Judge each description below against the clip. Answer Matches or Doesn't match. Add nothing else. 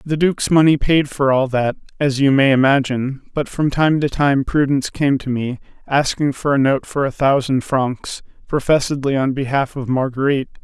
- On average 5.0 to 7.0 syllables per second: Matches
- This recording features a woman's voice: Doesn't match